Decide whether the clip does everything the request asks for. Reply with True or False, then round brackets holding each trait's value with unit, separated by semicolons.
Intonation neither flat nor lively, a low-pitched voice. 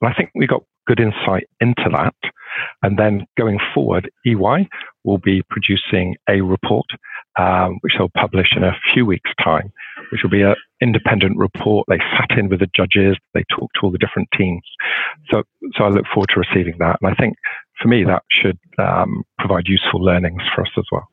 False (2.3 semitones; 100 Hz)